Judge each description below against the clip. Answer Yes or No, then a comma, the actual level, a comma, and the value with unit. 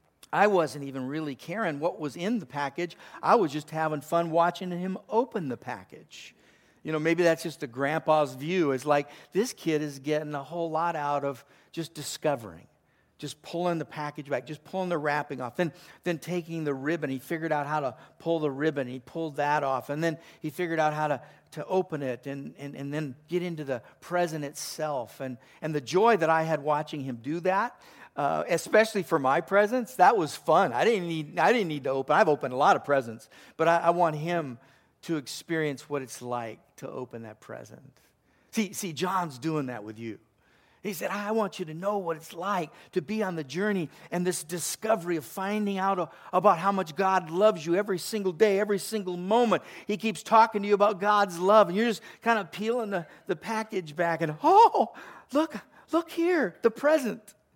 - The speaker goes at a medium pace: No, fast, 215 wpm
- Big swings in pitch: No, average, 4.7 semitones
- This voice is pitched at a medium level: Yes, medium, 165 Hz